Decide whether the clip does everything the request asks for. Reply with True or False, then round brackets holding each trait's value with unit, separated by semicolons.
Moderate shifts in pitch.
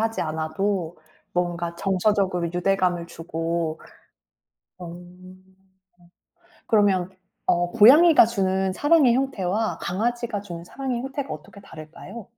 True (4.7 semitones)